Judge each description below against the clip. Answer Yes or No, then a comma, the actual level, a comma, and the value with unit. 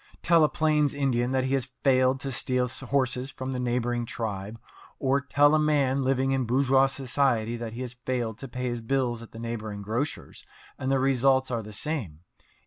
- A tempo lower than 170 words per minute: No, average, 195 wpm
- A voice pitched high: No, low, 130 Hz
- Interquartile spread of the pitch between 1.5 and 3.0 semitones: Yes, narrow, 2.4 semitones